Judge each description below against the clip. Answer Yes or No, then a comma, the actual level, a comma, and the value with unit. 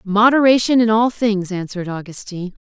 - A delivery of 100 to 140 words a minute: Yes, slow, 135 wpm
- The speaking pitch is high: Yes, high, 210 Hz